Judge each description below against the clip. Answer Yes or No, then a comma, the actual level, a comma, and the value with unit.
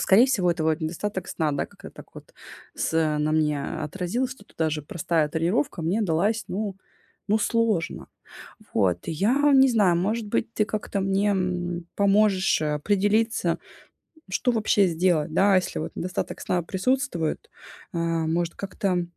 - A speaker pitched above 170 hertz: Yes, medium, 185 Hz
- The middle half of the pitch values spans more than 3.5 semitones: Yes, average, 4.3 semitones